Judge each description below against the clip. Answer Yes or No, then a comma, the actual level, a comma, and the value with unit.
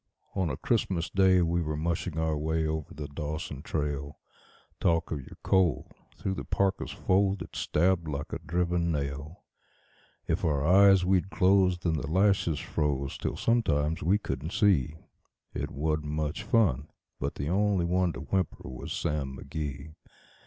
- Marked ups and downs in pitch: No, average, 3.9 semitones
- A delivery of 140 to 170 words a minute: Yes, average, 160 wpm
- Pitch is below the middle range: Yes, very low, 80 Hz